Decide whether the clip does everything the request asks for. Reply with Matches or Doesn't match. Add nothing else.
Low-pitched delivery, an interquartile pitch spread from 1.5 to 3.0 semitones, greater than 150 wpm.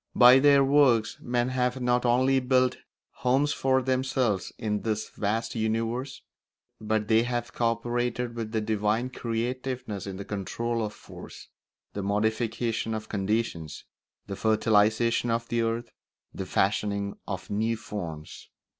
Doesn't match